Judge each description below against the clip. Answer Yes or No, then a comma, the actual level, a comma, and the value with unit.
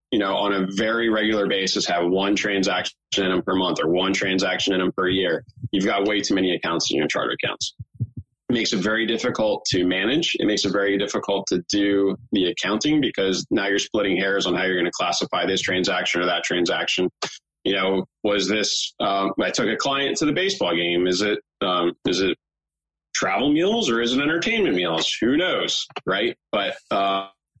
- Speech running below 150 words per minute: No, average, 200 wpm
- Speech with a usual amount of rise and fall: No, narrow, 2.1 semitones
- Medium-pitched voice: No, low, 100 Hz